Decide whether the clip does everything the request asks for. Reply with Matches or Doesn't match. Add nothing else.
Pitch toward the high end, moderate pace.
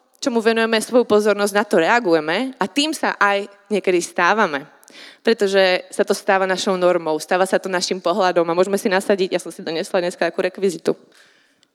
Doesn't match